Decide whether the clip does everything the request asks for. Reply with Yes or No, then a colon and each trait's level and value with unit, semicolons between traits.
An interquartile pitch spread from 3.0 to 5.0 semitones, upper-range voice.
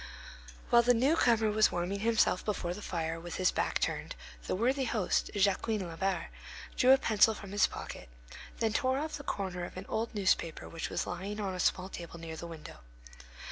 Yes: average, 4.3 semitones; high, 200 Hz